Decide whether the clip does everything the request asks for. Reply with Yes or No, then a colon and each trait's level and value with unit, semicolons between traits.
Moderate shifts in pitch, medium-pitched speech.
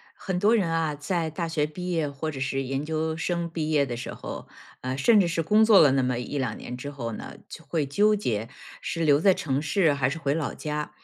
Yes: average, 3.5 semitones; medium, 155 Hz